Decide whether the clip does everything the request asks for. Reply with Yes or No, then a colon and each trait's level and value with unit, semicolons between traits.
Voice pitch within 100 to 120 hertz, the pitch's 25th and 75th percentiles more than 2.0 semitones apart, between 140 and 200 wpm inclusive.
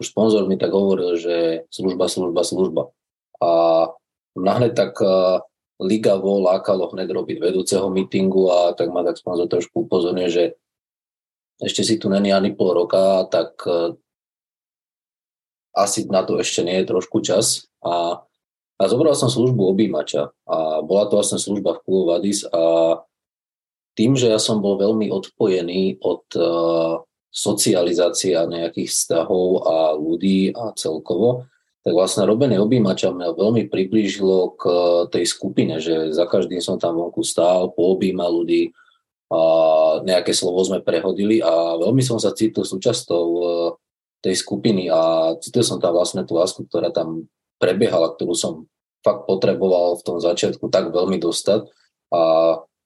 No: very low, 90 Hz; narrow, 2.6 semitones; average, 145 wpm